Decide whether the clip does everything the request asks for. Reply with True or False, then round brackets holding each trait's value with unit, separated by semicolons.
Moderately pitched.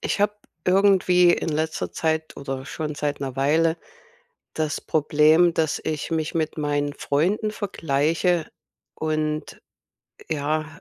True (155 Hz)